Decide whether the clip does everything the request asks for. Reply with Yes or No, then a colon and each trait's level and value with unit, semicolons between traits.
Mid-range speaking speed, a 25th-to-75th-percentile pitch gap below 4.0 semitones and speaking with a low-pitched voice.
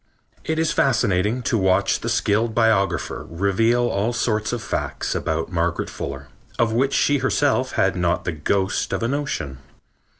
No: average, 160 wpm; average, 4.8 semitones; low, 110 Hz